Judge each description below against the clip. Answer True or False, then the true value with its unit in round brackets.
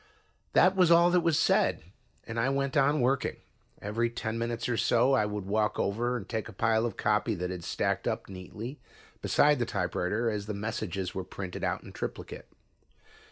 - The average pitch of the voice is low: True (115 Hz)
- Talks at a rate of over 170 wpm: True (190 wpm)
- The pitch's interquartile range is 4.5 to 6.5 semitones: False (4.0 semitones)